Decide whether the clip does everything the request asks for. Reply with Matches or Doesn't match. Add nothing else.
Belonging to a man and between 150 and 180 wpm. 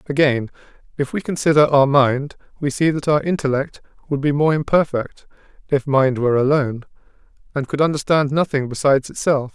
Matches